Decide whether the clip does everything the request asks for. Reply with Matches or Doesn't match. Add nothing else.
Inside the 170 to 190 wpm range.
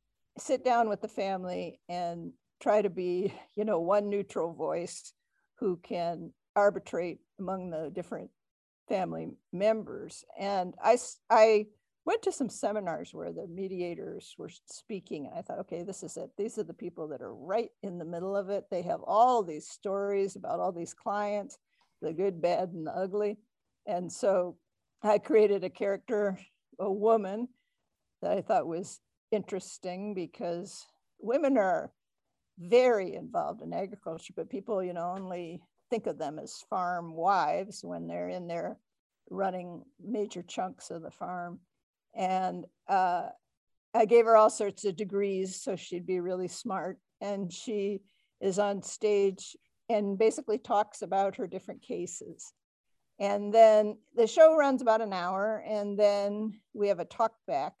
Doesn't match